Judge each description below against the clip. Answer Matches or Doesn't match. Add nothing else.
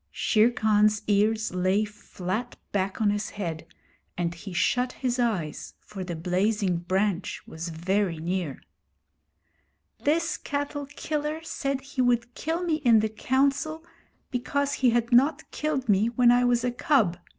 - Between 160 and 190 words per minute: Doesn't match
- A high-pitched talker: Matches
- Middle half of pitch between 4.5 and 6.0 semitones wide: Matches